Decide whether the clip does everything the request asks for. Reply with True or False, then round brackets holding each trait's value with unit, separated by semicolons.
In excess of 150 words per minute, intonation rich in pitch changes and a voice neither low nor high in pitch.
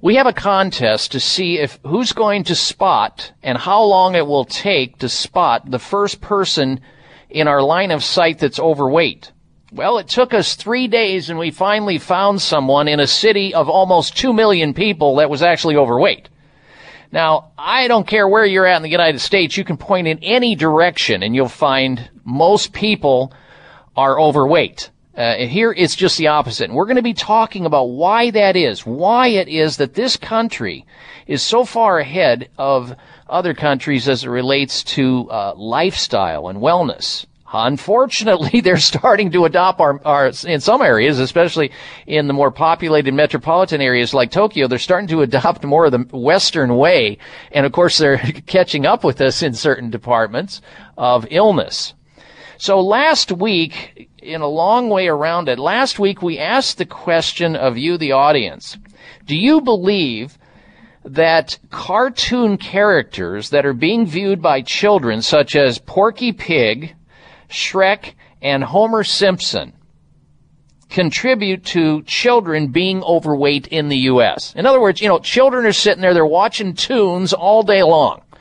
True (165 wpm; 6.1 semitones; 170 Hz)